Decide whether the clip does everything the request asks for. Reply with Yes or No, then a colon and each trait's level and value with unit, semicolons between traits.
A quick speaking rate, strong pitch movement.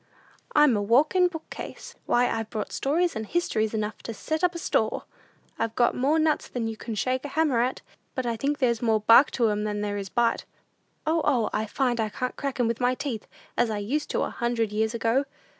No: fast, 225 wpm; average, 4.3 semitones